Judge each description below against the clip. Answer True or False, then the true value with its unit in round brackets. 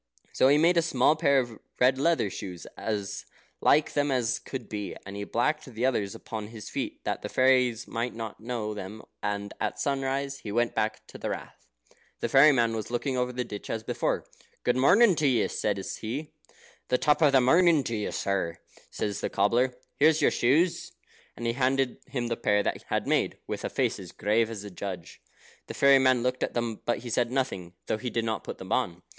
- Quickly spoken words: True (215 wpm)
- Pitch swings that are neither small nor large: True (4.0 semitones)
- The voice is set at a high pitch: False (120 Hz)